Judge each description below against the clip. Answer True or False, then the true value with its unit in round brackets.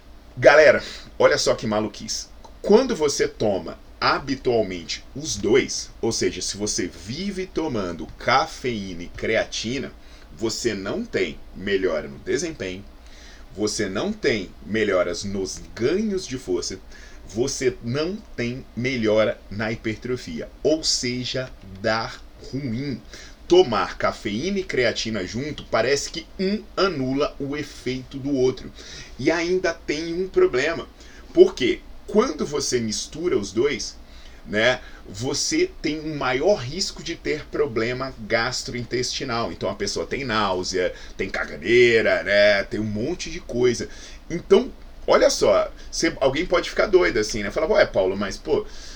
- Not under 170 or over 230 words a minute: False (130 wpm)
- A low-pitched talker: True (130 Hz)